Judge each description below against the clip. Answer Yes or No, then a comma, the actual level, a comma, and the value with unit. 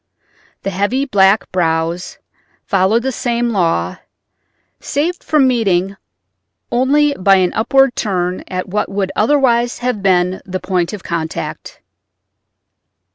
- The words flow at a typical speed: No, slow, 120 wpm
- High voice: Yes, high, 200 Hz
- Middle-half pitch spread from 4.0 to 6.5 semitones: Yes, average, 5.1 semitones